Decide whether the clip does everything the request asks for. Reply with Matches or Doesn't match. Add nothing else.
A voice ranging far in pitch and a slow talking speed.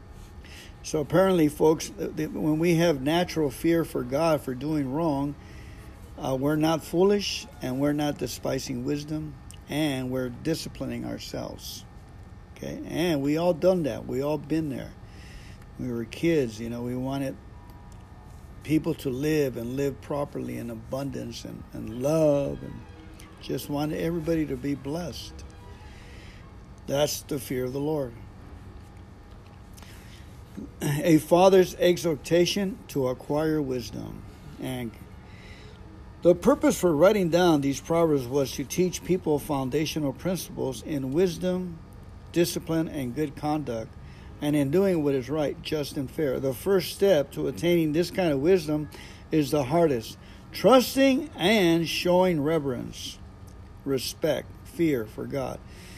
Matches